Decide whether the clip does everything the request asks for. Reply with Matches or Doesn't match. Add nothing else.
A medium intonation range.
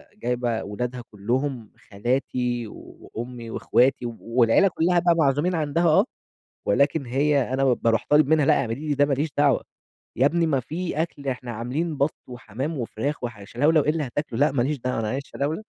Matches